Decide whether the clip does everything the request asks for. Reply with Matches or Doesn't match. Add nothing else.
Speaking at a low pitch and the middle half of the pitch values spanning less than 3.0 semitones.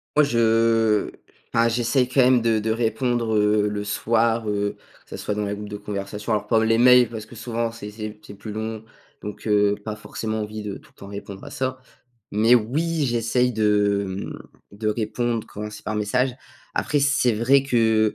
Matches